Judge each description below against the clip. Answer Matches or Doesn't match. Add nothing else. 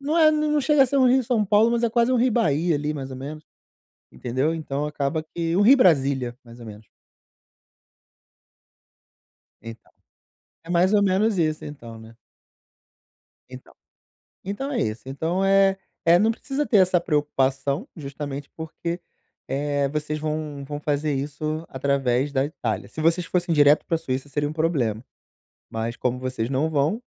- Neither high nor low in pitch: Matches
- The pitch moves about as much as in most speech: Doesn't match